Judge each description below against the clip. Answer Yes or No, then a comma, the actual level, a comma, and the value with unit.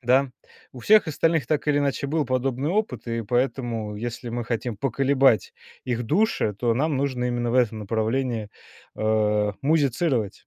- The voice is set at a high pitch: No, low, 125 Hz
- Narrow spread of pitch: No, average, 3.3 semitones